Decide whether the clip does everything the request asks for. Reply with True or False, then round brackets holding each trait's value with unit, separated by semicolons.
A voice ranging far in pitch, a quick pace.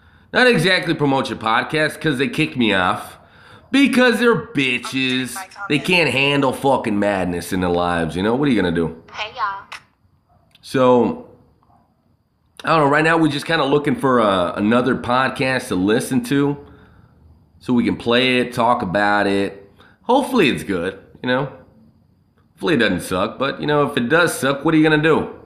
False (6.9 semitones; 185 wpm)